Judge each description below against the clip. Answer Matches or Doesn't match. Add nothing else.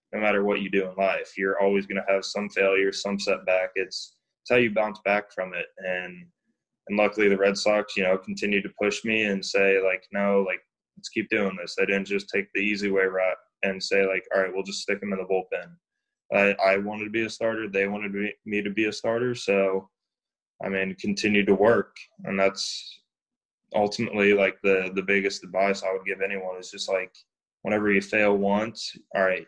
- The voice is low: Matches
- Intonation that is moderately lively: Doesn't match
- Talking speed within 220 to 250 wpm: Matches